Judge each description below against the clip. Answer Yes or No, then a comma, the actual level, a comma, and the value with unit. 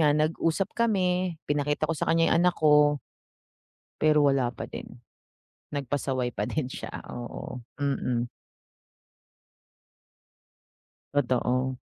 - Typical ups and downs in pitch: Yes, average, 3.8 semitones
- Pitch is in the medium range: Yes, medium, 145 Hz